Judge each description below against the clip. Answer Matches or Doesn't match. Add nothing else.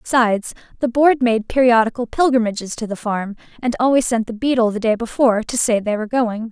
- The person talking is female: Matches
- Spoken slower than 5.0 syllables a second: Doesn't match